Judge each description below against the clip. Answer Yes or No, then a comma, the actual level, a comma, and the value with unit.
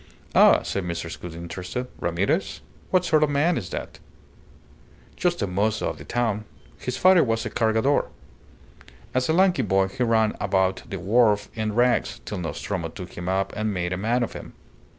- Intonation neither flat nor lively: Yes, average, 4.9 semitones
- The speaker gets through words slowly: No, average, 180 wpm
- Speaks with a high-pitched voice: No, low, 110 Hz